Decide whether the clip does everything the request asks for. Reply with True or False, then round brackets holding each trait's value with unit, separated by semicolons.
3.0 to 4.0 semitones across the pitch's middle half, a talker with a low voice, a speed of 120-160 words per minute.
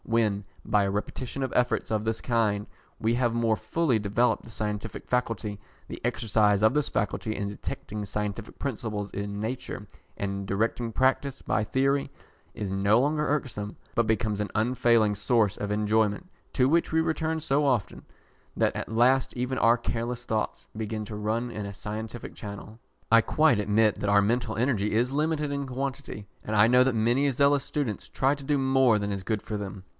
False (3.7 semitones; 115 Hz; 185 wpm)